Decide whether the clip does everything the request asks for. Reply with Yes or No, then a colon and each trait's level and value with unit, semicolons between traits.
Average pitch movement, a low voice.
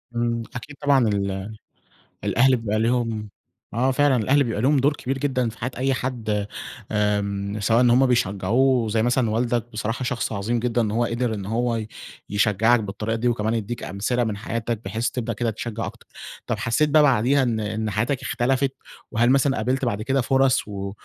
Yes: average, 3.0 semitones; low, 115 Hz